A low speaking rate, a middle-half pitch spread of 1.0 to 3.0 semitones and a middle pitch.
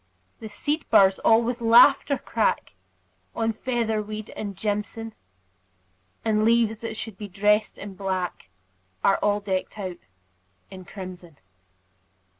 No: slow, 120 wpm; narrow, 2.5 semitones; high, 215 Hz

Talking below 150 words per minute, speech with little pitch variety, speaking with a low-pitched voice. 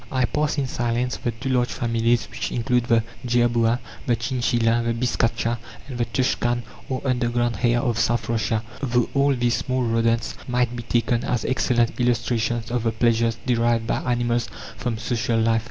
No: average, 170 wpm; narrow, 1.0 semitones; low, 120 Hz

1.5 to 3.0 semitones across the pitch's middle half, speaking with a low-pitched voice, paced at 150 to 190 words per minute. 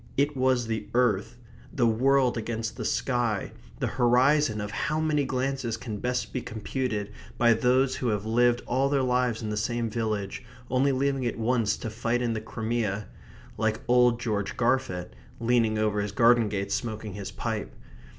Yes: average, 2.7 semitones; low, 120 Hz; average, 170 wpm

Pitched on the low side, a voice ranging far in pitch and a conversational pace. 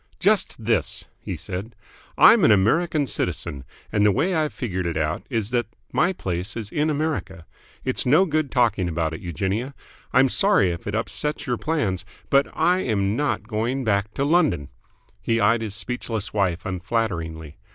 Yes: low, 110 Hz; wide, 7.1 semitones; average, 170 wpm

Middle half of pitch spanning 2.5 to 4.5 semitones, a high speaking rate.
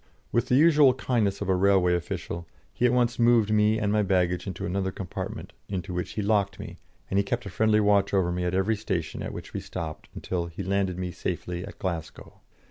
Yes: average, 3.2 semitones; fast, 215 wpm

